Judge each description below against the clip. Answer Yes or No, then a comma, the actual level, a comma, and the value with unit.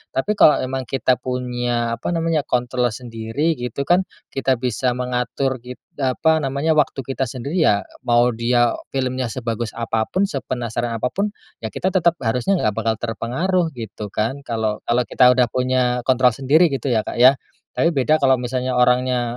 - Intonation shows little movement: Yes, narrow, 2.3 semitones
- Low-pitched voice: Yes, low, 125 Hz